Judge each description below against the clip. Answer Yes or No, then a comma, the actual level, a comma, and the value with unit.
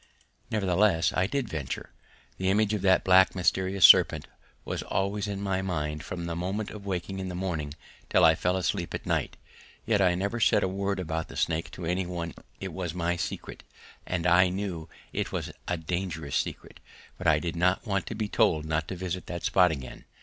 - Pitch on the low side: Yes, very low, 90 Hz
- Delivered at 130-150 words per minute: No, average, 200 wpm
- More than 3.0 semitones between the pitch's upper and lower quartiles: No, narrow, 2.4 semitones